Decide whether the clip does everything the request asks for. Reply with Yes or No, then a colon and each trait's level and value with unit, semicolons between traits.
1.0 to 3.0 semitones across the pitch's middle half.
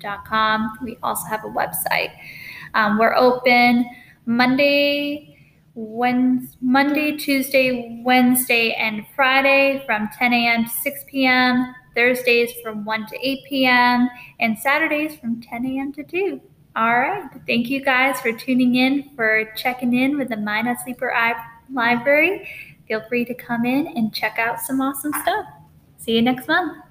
Yes: average, 2.7 semitones